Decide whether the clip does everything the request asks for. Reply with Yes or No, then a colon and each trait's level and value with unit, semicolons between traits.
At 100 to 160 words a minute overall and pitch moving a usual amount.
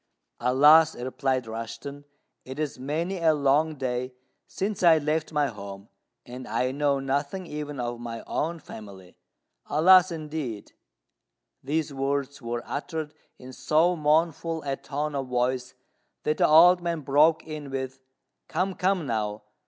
Yes: average, 140 wpm; average, 3.9 semitones